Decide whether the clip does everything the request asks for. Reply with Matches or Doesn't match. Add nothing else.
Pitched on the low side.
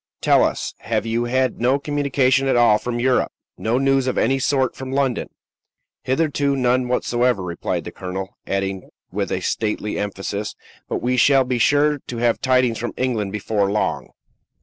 Matches